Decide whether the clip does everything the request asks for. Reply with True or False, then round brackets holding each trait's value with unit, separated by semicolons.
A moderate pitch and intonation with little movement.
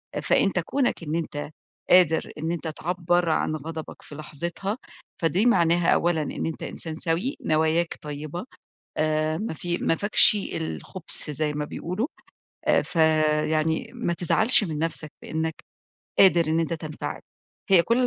True (165 Hz; 2.3 semitones)